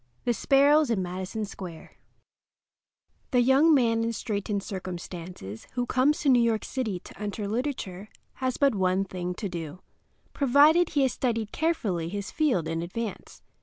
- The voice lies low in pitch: No, high, 220 Hz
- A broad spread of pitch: Yes, wide, 6.0 semitones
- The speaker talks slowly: No, average, 155 wpm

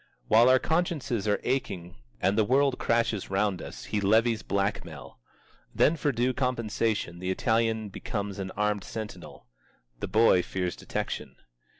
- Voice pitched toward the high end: No, low, 110 Hz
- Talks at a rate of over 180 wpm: No, average, 145 wpm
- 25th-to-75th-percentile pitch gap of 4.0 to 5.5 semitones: No, average, 3.5 semitones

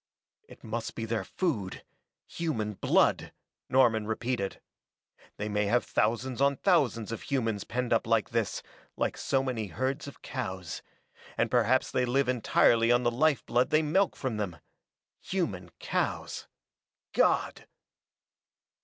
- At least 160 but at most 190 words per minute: No, slow, 135 wpm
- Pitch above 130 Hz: No, low, 120 Hz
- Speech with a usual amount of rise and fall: Yes, average, 3.4 semitones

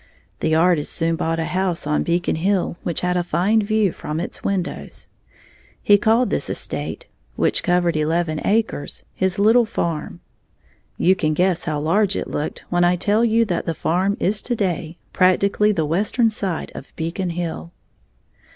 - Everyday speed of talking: Yes, average, 170 wpm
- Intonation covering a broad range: No, average, 3.6 semitones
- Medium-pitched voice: Yes, medium, 180 Hz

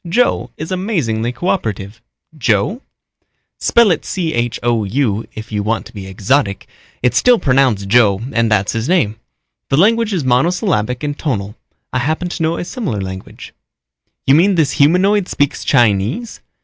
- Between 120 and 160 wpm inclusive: Yes, average, 150 wpm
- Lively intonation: Yes, wide, 8.3 semitones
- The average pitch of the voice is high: No, low, 130 Hz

